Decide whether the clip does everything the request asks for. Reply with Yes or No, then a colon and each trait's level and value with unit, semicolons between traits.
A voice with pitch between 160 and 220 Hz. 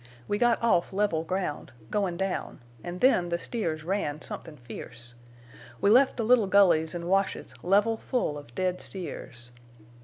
Yes: medium, 185 Hz